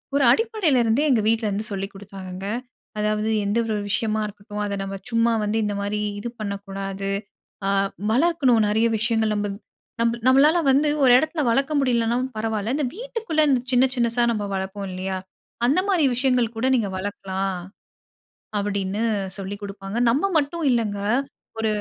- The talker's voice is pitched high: Yes, high, 220 Hz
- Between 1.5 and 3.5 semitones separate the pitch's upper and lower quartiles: No, average, 4.3 semitones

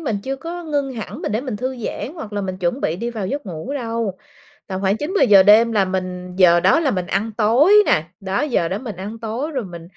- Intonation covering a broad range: Yes, wide, 5.7 semitones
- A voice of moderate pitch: No, high, 220 Hz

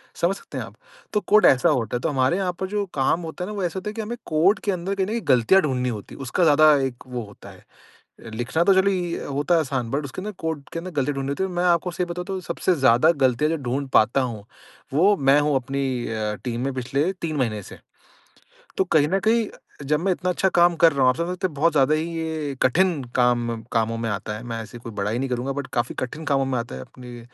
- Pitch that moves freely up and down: Yes, wide, 6.0 semitones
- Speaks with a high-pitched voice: No, medium, 145 Hz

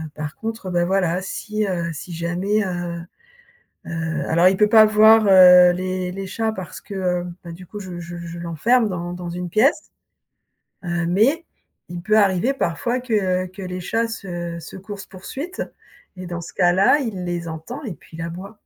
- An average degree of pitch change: Yes, average, 3.5 semitones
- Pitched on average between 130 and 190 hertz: Yes, medium, 185 Hz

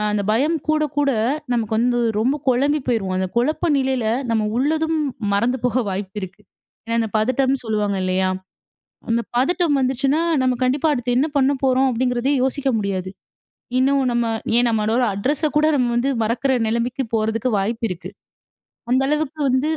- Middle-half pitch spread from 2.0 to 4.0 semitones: Yes, average, 3.7 semitones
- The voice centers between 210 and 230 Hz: No, very high, 250 Hz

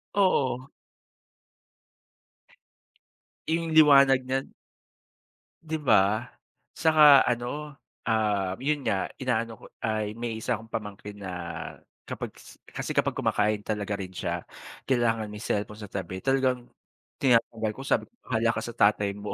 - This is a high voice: No, low, 115 Hz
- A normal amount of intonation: Yes, average, 4.0 semitones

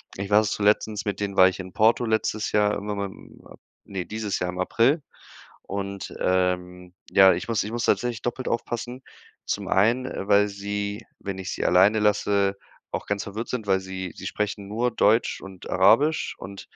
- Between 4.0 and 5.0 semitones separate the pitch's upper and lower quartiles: No, narrow, 2.4 semitones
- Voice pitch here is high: No, low, 100 Hz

